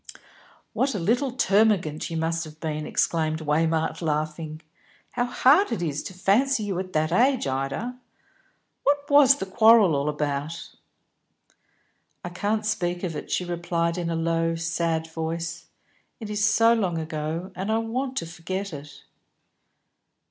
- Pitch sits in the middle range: Yes, medium, 170 Hz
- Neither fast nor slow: Yes, average, 150 wpm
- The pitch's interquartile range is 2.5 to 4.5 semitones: No, average, 5.2 semitones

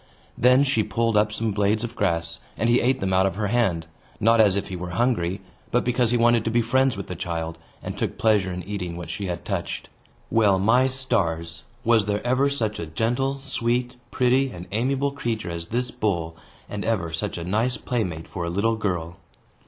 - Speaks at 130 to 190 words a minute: No, fast, 205 wpm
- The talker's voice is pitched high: No, low, 110 Hz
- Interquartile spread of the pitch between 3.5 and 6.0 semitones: Yes, average, 5.2 semitones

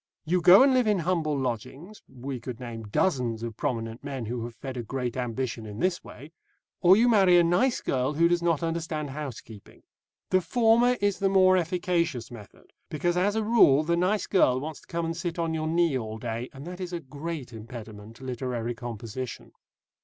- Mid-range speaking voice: Yes, medium, 150 Hz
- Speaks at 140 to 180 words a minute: No, average, 200 wpm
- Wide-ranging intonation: Yes, wide, 6.6 semitones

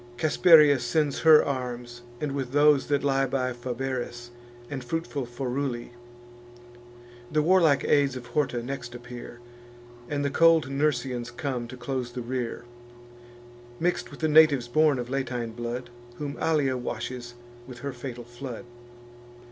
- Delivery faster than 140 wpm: No, slow, 135 wpm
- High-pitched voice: No, low, 130 Hz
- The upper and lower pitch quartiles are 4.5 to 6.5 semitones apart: No, average, 3.0 semitones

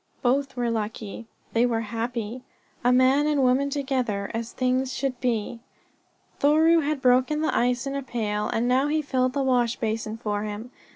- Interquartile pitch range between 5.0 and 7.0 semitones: No, average, 3.1 semitones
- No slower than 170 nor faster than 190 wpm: Yes, average, 175 wpm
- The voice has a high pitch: Yes, very high, 250 Hz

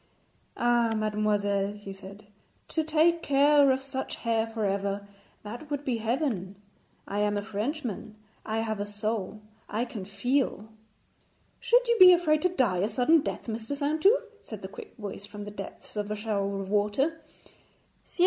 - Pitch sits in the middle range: No, high, 220 Hz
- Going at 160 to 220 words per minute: Yes, average, 170 wpm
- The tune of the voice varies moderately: No, wide, 5.7 semitones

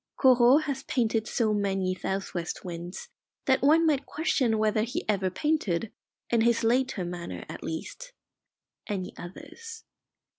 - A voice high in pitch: Yes, high, 225 Hz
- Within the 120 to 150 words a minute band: Yes, average, 140 wpm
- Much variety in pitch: Yes, wide, 6.2 semitones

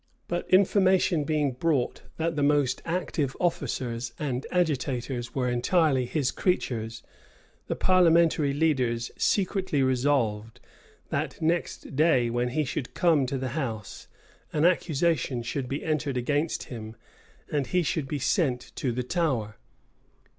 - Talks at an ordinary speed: No, slow, 130 wpm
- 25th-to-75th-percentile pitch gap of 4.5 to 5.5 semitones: Yes, average, 4.9 semitones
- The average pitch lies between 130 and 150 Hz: Yes, medium, 140 Hz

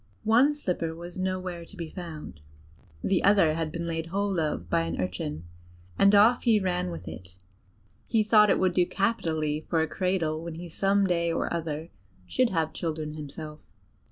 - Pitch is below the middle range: No, medium, 170 Hz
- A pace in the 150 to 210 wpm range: Yes, average, 180 wpm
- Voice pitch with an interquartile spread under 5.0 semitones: Yes, average, 3.7 semitones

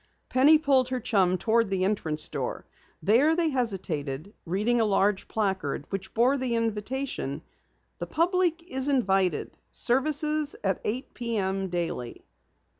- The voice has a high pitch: Yes, high, 225 Hz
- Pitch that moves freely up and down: Yes, wide, 5.7 semitones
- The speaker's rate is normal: No, slow, 130 wpm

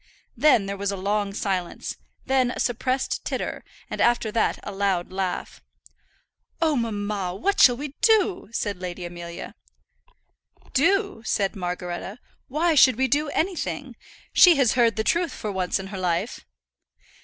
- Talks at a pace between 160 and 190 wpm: No, average, 150 wpm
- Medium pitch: No, high, 215 Hz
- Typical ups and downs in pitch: No, wide, 6.0 semitones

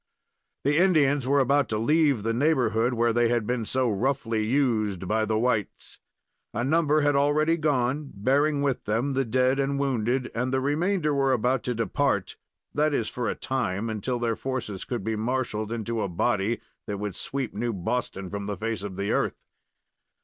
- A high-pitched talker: No, low, 125 Hz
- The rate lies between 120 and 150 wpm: No, average, 185 wpm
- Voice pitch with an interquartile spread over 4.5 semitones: No, average, 4.2 semitones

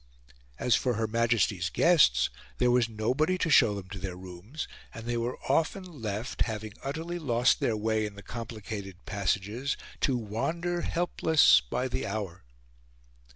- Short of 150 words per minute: No, average, 155 wpm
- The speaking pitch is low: Yes, low, 115 Hz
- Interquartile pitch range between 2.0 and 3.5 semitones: No, average, 5.3 semitones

